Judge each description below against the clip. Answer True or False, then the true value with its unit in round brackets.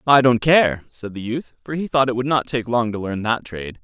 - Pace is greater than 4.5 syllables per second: True (5.3 syllables/s)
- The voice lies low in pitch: True (120 Hz)